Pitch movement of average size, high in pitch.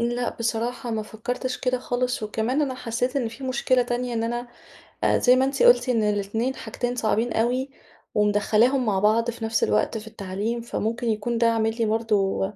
No: narrow, 2.1 semitones; high, 230 Hz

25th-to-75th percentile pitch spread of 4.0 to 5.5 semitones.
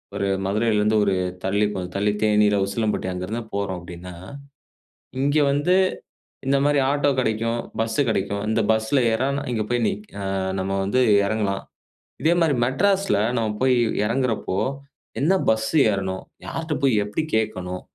Yes: average, 5.1 semitones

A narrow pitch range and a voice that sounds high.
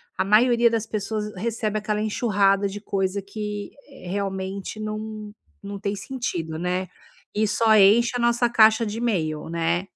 Yes: narrow, 2.2 semitones; high, 210 Hz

